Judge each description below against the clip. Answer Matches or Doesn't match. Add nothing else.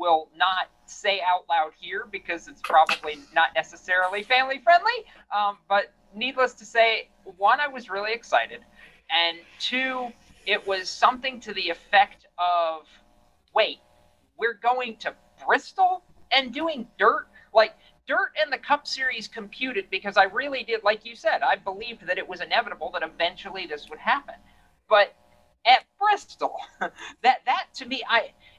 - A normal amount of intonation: Doesn't match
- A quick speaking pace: Doesn't match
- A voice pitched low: Doesn't match